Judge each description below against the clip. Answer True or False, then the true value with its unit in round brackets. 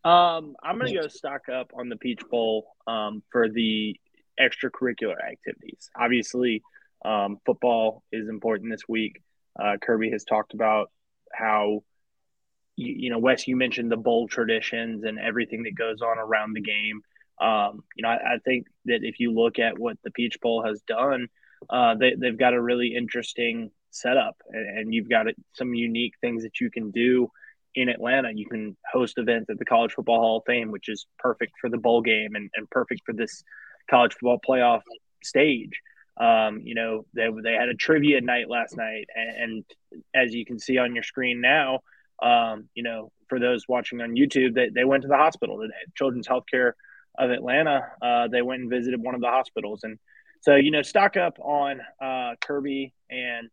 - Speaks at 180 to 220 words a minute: True (190 wpm)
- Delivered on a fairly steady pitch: True (2.0 semitones)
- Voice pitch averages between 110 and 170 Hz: True (120 Hz)